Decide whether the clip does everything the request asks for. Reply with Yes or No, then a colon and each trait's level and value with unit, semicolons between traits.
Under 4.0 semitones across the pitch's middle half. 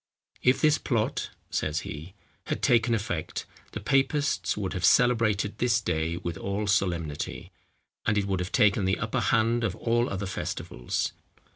No: average, 4.4 semitones